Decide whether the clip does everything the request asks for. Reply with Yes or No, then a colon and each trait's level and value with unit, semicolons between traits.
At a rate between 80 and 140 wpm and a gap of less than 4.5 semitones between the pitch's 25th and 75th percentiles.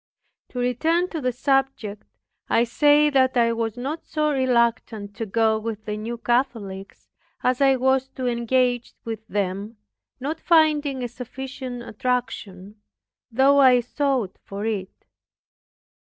Yes: slow, 135 wpm; average, 3.3 semitones